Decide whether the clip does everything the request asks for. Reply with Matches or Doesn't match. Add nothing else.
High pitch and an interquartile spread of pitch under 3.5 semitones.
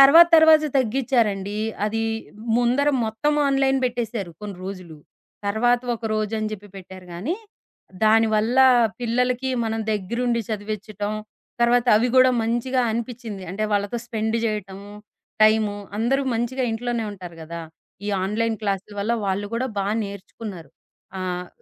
Matches